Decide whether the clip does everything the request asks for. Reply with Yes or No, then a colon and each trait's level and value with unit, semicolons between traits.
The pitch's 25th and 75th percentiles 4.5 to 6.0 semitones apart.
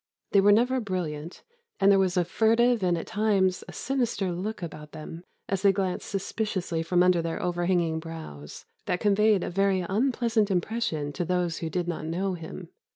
No: average, 3.4 semitones